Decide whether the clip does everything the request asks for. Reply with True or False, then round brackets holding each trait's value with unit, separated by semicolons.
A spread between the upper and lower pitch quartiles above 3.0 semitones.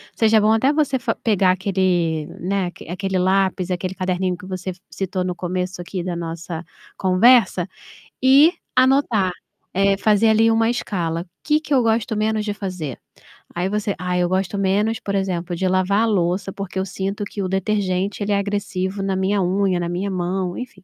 False (2.5 semitones)